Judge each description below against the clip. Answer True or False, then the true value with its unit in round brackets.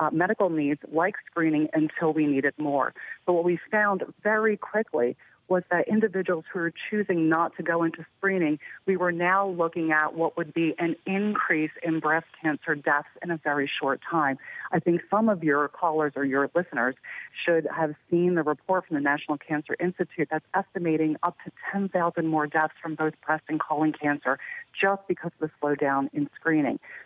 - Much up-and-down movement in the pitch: False (2.8 semitones)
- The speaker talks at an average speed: True (185 wpm)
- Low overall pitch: False (165 Hz)